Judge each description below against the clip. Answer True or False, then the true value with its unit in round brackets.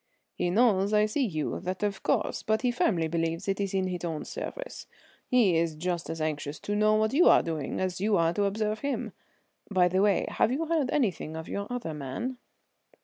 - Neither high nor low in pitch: False (195 Hz)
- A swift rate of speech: True (210 wpm)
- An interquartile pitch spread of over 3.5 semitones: True (4.6 semitones)